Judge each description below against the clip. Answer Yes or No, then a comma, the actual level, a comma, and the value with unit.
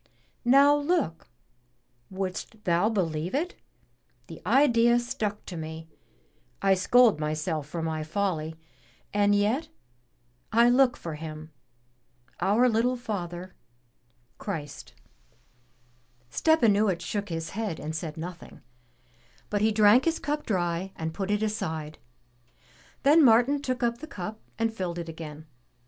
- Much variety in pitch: Yes, wide, 6.4 semitones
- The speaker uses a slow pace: Yes, slow, 130 wpm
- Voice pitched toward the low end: No, high, 200 Hz